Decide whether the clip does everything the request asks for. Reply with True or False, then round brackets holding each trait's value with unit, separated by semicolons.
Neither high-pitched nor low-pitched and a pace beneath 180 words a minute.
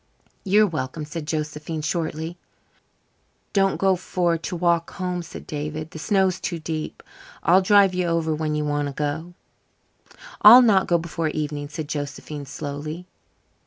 True (160 Hz; 160 wpm)